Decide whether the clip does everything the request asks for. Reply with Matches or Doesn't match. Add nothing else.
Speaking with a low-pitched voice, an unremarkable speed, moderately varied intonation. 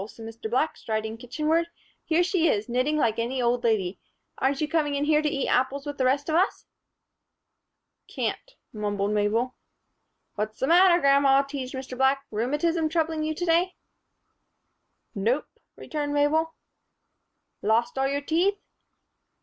Doesn't match